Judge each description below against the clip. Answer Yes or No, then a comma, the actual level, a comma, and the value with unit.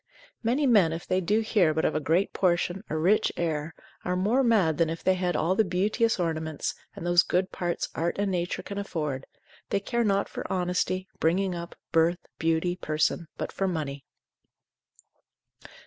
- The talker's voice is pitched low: No, medium, 180 Hz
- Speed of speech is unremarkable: Yes, average, 180 wpm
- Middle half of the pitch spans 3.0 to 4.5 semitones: Yes, average, 3.4 semitones